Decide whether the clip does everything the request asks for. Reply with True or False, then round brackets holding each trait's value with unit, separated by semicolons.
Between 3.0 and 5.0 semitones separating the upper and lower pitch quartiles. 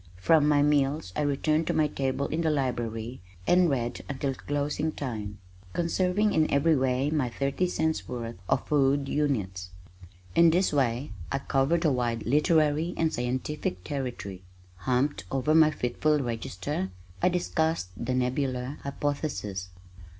True (3.8 semitones)